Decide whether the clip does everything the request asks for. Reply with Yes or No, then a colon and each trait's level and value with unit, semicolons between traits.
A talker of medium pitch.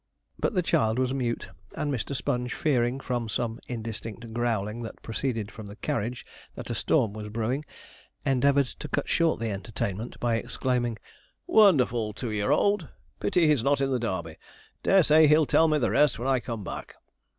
No: low, 120 Hz